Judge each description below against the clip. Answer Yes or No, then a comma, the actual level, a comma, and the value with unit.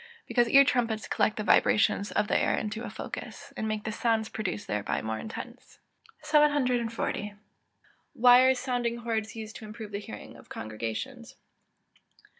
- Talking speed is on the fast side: No, average, 160 wpm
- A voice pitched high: Yes, high, 220 Hz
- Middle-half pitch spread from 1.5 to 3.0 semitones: Yes, average, 2.7 semitones